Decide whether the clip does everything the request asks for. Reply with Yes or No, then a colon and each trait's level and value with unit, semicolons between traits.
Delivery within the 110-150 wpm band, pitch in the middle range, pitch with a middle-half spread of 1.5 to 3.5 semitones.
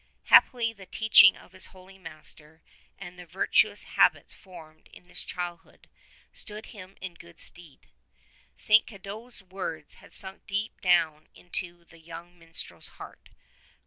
Yes: average, 140 wpm; medium, 180 Hz; average, 2.8 semitones